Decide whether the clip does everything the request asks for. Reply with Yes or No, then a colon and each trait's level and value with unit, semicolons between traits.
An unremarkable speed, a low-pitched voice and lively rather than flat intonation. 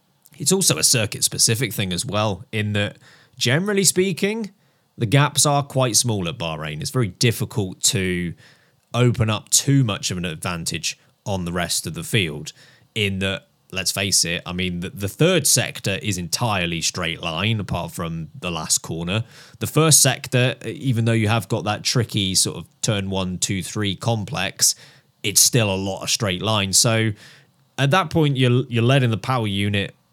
Yes: average, 175 wpm; low, 115 Hz; wide, 5.8 semitones